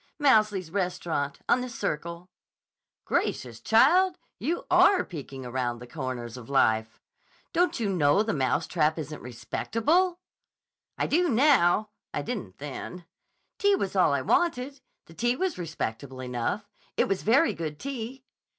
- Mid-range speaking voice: Yes, medium, 180 Hz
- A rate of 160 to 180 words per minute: No, average, 140 wpm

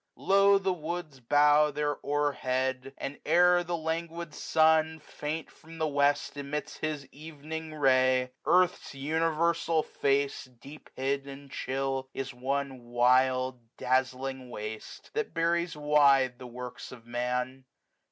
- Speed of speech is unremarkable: No, slow, 130 wpm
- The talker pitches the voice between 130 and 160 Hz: Yes, medium, 140 Hz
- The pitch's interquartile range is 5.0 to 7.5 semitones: No, average, 3.5 semitones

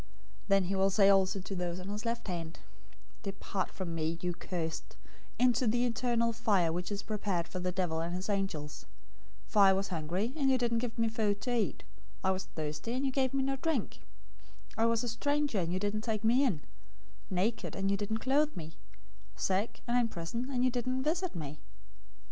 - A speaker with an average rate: No, fast, 210 wpm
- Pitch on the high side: Yes, high, 205 Hz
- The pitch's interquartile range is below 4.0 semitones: No, average, 4.8 semitones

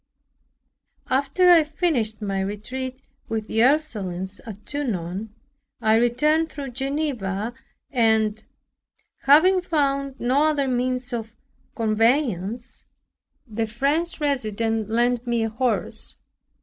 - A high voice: Yes, high, 240 Hz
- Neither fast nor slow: No, slow, 105 wpm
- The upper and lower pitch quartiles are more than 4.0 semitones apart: Yes, average, 4.4 semitones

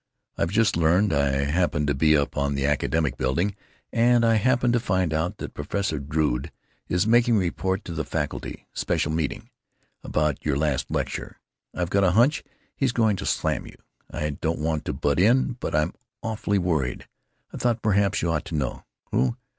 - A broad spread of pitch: Yes, wide, 6.0 semitones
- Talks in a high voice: No, very low, 85 Hz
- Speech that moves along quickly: No, average, 180 wpm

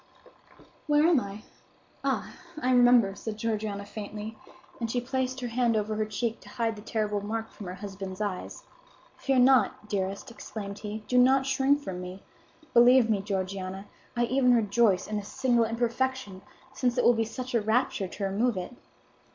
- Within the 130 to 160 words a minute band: No, average, 175 wpm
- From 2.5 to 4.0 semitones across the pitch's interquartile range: Yes, average, 3.5 semitones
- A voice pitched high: Yes, high, 225 Hz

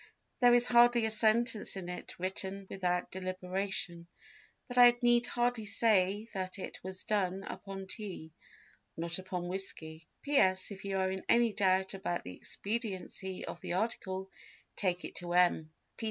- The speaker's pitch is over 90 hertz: Yes, high, 190 Hz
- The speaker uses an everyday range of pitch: Yes, average, 3.1 semitones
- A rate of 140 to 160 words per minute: Yes, average, 155 wpm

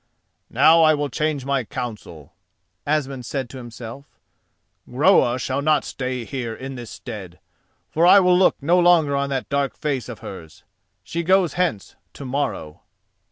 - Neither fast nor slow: Yes, average, 160 wpm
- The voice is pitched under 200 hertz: Yes, low, 135 Hz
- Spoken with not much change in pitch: No, average, 4.1 semitones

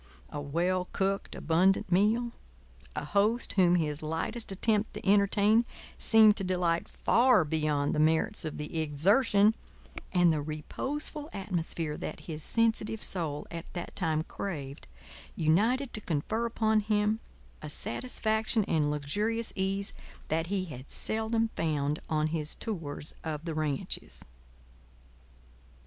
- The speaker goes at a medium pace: No, slow, 130 wpm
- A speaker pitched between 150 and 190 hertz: Yes, medium, 185 Hz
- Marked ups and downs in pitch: Yes, wide, 5.7 semitones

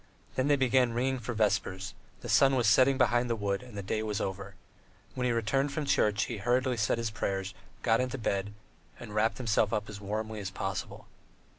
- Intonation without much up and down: No, average, 3.7 semitones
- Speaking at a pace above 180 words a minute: Yes, average, 200 wpm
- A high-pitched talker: No, low, 110 Hz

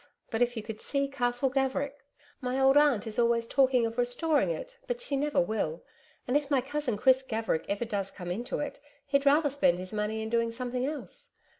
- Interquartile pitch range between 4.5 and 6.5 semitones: No, average, 3.8 semitones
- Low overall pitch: No, very high, 250 Hz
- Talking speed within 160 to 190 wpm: No, fast, 205 wpm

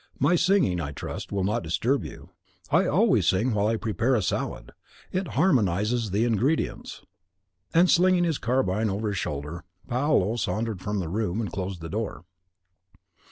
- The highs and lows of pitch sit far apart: Yes, wide, 5.7 semitones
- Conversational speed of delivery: Yes, average, 160 wpm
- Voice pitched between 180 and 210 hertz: No, low, 110 Hz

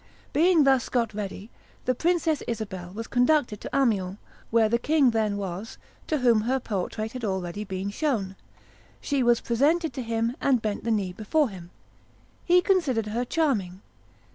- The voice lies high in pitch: Yes, high, 230 Hz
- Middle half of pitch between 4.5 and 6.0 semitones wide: Yes, average, 5.2 semitones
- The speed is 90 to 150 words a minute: No, average, 165 wpm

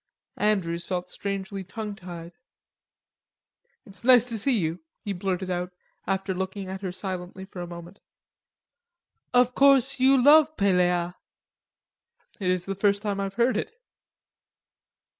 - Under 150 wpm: Yes, slow, 135 wpm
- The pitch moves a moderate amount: Yes, average, 3.2 semitones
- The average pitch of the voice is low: No, high, 195 Hz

